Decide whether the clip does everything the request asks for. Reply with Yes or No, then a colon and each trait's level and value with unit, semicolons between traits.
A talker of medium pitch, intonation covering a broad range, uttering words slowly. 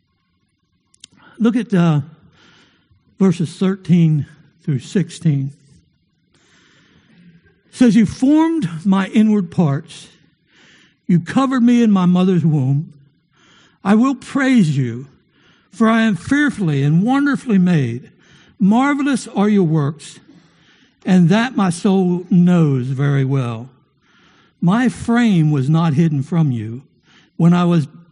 Yes: medium, 175 Hz; wide, 5.9 semitones; slow, 115 wpm